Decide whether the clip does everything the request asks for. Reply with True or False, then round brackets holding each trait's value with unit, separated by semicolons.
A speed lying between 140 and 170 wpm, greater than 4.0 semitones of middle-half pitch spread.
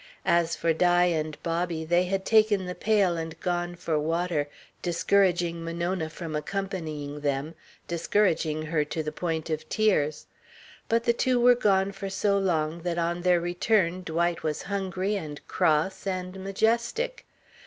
False (155 wpm; 3.2 semitones)